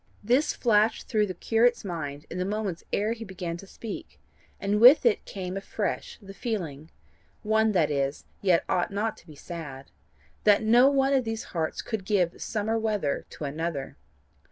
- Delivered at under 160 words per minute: No, average, 180 wpm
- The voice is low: No, high, 200 Hz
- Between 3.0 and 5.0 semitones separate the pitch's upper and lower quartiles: Yes, average, 4.7 semitones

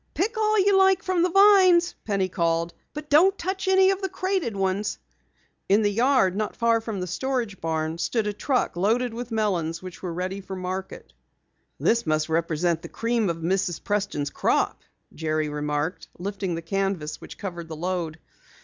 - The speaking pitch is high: Yes, high, 195 Hz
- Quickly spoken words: No, average, 180 wpm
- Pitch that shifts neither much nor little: No, wide, 7.7 semitones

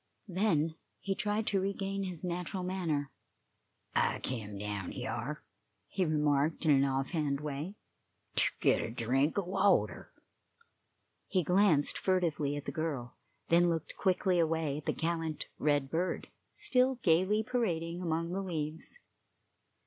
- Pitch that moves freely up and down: No, average, 4.3 semitones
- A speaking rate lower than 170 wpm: Yes, average, 140 wpm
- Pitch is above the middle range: No, medium, 165 Hz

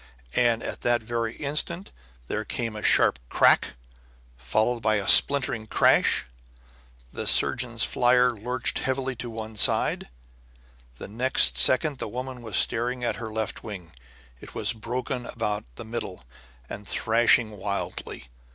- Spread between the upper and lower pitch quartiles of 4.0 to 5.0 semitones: No, narrow, 2.5 semitones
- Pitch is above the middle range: No, low, 115 Hz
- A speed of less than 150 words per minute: Yes, slow, 135 wpm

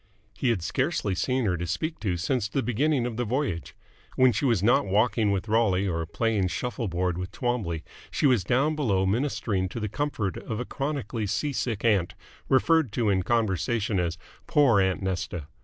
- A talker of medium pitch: No, low, 110 Hz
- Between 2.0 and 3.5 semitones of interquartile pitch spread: No, average, 5.2 semitones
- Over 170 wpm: Yes, average, 190 wpm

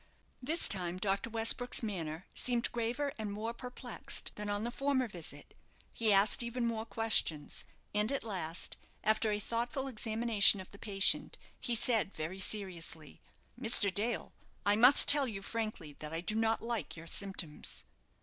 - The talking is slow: No, average, 160 wpm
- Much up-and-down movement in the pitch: No, average, 3.5 semitones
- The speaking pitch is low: No, high, 215 Hz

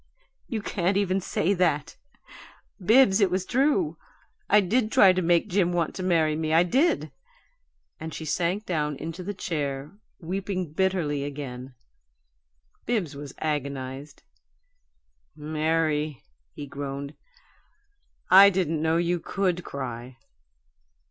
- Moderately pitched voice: Yes, medium, 165 Hz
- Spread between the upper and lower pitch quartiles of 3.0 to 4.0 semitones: No, average, 4.4 semitones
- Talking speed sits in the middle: No, slow, 120 wpm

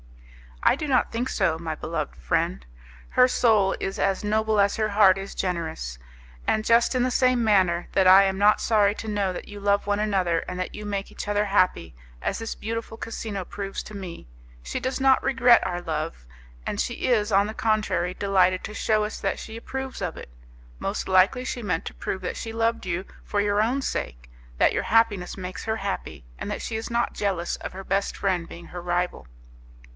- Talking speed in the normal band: No, fast, 210 wpm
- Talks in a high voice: Yes, high, 200 Hz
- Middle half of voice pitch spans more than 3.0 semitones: Yes, average, 3.4 semitones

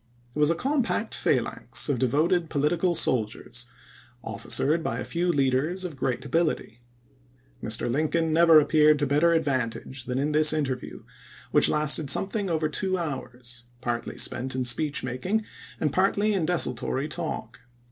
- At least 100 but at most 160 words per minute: Yes, average, 150 wpm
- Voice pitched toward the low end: No, medium, 150 Hz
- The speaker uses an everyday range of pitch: Yes, average, 4.5 semitones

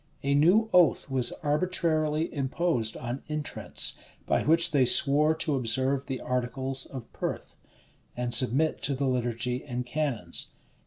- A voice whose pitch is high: No, low, 135 Hz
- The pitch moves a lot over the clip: No, average, 3.6 semitones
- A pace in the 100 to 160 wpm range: Yes, average, 145 wpm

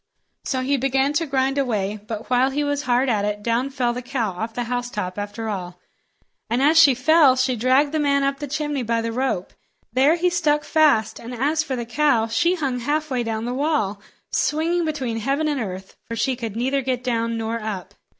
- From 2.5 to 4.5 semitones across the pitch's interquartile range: Yes, average, 4.1 semitones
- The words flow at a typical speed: No, fast, 210 wpm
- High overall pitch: Yes, very high, 255 Hz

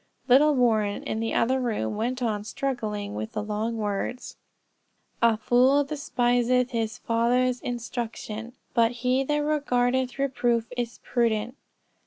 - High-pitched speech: Yes, high, 240 Hz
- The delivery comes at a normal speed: No, slow, 130 wpm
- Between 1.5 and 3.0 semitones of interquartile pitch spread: Yes, narrow, 2.4 semitones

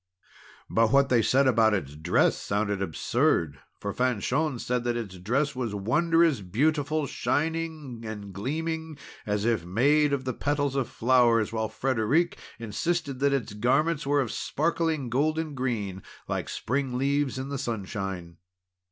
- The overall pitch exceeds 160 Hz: No, low, 130 Hz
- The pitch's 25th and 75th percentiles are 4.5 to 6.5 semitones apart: Yes, average, 5.1 semitones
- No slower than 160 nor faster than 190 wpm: No, average, 145 wpm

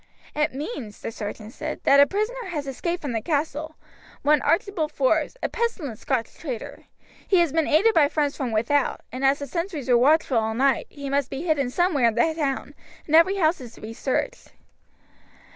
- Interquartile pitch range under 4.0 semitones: No, average, 4.3 semitones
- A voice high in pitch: Yes, very high, 290 Hz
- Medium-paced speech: Yes, average, 195 wpm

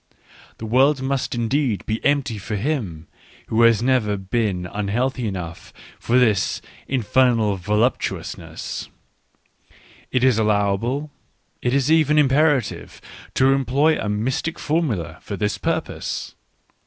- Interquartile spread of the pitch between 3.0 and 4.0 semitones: No, average, 4.7 semitones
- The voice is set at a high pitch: No, low, 120 Hz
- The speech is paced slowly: Yes, slow, 130 wpm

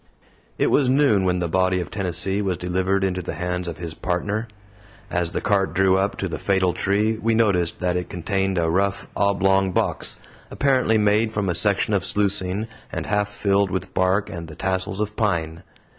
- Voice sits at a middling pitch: No, very low, 95 Hz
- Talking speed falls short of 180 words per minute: No, average, 190 wpm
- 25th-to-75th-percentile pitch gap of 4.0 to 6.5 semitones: No, narrow, 2.4 semitones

